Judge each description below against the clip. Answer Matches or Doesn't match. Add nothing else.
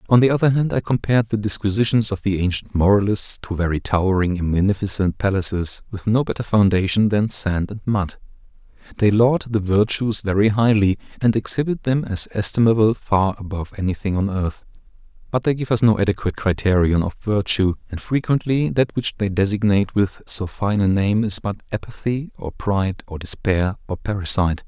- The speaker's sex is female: Doesn't match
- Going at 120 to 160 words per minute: Doesn't match